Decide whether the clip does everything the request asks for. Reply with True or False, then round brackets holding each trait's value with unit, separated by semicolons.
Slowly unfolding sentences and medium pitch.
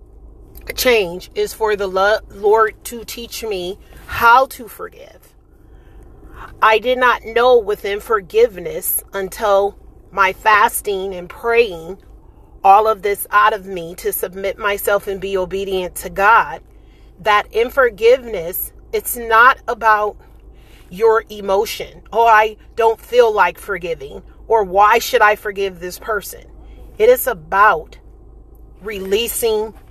False (120 wpm; 220 Hz)